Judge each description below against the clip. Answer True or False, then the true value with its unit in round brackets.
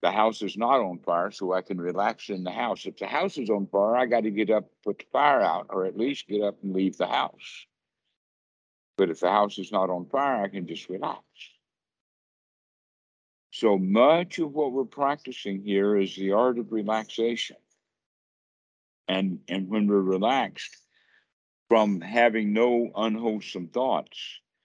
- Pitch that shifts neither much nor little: True (3.4 semitones)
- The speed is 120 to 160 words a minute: False (175 wpm)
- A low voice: True (105 Hz)